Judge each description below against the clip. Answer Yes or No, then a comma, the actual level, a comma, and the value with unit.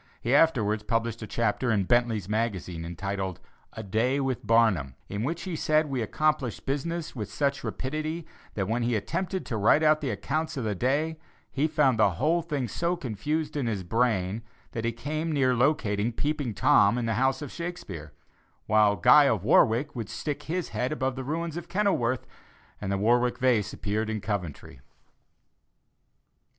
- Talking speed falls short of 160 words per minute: No, average, 175 wpm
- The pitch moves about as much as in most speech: No, wide, 6.0 semitones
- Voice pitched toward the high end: No, low, 120 Hz